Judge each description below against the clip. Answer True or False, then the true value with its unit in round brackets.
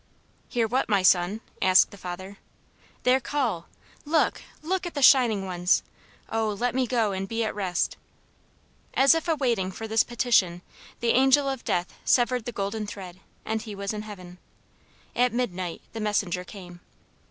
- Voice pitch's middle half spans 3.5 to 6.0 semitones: True (4.8 semitones)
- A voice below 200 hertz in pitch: False (215 Hz)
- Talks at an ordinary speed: True (165 wpm)